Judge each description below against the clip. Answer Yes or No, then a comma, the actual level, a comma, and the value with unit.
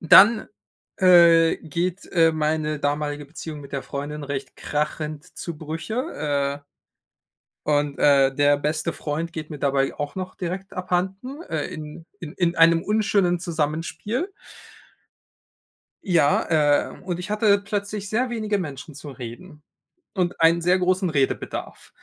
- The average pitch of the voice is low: No, medium, 165 Hz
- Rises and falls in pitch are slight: No, average, 4.0 semitones